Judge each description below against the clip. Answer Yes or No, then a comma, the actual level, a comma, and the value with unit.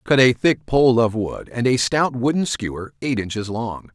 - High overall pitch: No, low, 120 Hz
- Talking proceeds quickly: Yes, fast, 215 wpm